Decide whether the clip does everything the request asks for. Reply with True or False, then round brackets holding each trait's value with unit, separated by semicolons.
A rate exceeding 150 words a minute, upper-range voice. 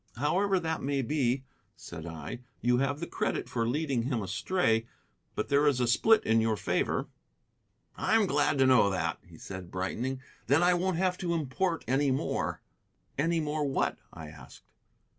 False (170 wpm; 135 Hz)